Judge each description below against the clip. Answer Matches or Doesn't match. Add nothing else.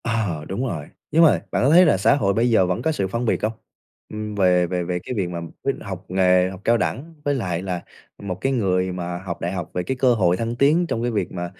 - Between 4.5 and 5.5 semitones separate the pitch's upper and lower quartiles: Matches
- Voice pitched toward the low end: Matches